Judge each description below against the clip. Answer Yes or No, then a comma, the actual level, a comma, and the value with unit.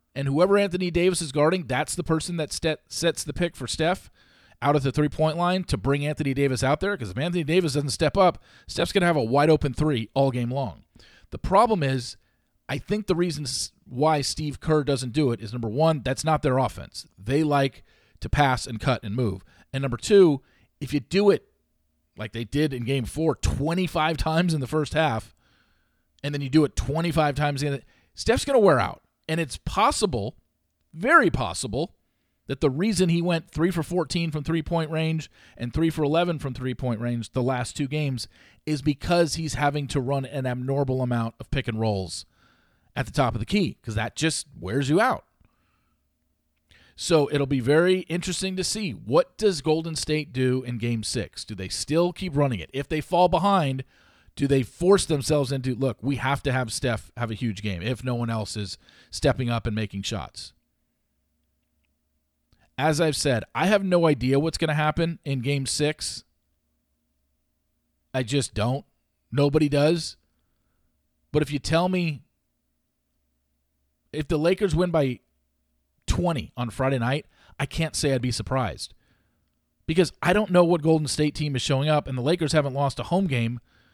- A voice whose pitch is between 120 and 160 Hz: Yes, medium, 140 Hz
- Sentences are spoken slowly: No, average, 190 wpm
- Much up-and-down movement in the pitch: Yes, wide, 5.8 semitones